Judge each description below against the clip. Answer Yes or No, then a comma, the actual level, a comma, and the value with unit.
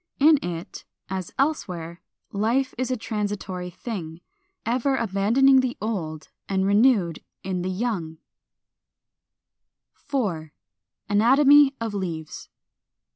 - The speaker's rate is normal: No, slow, 105 wpm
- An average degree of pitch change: No, wide, 6.2 semitones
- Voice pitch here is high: Yes, high, 205 Hz